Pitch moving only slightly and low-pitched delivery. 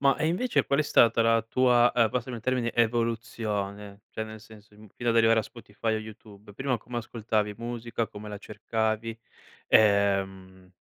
Yes: narrow, 2.2 semitones; low, 110 Hz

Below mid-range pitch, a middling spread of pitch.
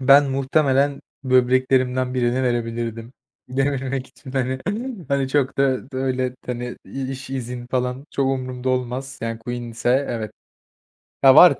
No: low, 130 Hz; narrow, 1.4 semitones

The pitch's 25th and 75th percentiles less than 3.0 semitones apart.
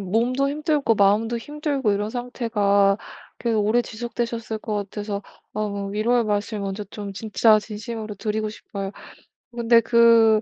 Yes: narrow, 2.4 semitones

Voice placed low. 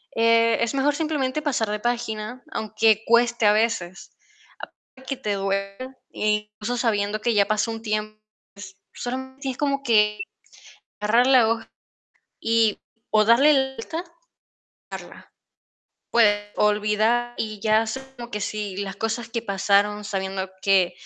No: high, 225 Hz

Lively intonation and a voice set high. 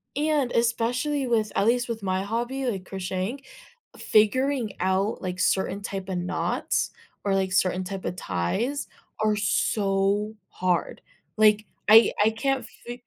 No: average, 4.0 semitones; high, 210 Hz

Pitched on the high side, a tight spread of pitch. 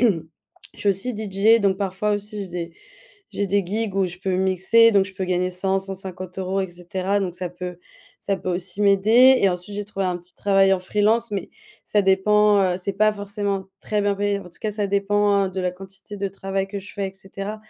Yes: high, 195 Hz; narrow, 1.7 semitones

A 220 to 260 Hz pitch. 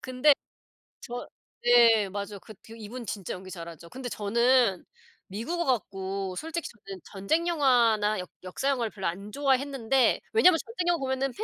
Yes: high, 235 Hz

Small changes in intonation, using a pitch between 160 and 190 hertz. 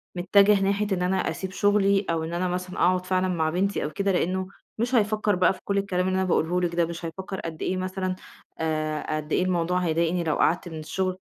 Yes: narrow, 2.2 semitones; medium, 185 Hz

